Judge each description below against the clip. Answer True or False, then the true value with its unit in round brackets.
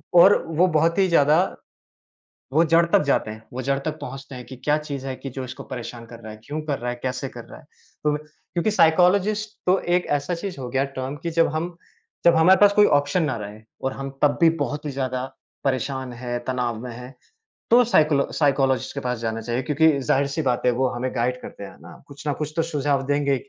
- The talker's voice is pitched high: False (140 Hz)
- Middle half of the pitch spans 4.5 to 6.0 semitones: False (4.0 semitones)